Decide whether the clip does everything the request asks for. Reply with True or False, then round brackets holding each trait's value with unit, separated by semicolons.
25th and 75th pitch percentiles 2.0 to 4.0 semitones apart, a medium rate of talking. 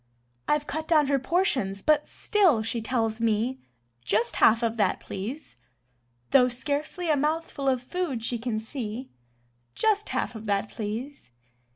False (5.2 semitones; 150 wpm)